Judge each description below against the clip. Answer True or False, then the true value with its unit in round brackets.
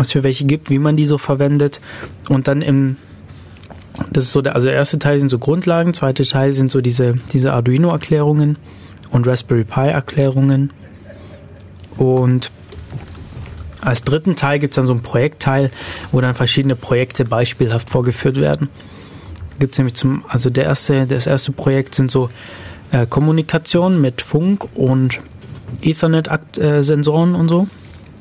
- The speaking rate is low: False (150 wpm)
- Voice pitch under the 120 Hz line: False (135 Hz)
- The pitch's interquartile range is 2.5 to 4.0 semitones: True (3.5 semitones)